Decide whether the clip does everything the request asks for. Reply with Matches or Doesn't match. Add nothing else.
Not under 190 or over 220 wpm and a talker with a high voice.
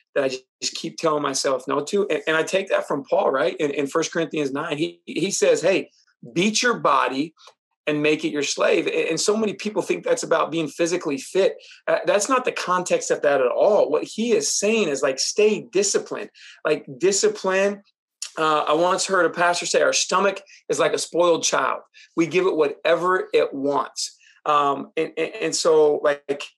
Matches